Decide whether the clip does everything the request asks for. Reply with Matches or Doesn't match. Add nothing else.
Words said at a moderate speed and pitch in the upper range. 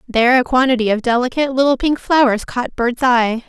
Matches